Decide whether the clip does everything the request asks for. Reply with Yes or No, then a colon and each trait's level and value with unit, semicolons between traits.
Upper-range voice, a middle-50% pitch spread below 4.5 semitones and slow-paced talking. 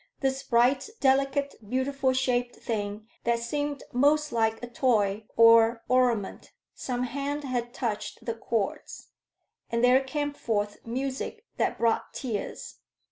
Yes: high, 245 Hz; average, 2.9 semitones; slow, 130 wpm